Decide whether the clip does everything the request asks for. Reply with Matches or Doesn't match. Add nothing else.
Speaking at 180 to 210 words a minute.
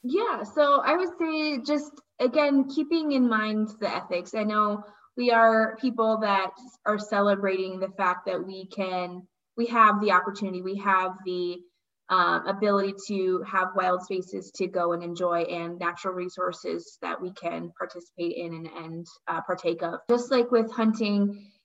Doesn't match